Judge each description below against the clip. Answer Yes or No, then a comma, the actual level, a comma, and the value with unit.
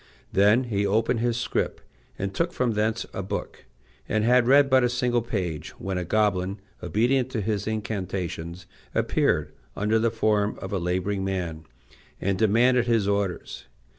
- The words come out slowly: No, average, 160 wpm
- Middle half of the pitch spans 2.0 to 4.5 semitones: Yes, average, 3.5 semitones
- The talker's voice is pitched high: No, low, 105 Hz